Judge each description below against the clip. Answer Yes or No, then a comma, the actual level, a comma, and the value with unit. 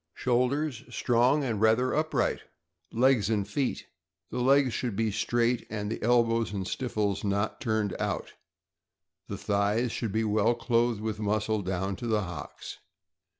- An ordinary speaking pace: Yes, average, 150 wpm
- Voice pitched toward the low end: Yes, low, 110 Hz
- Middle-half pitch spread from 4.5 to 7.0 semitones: No, average, 2.8 semitones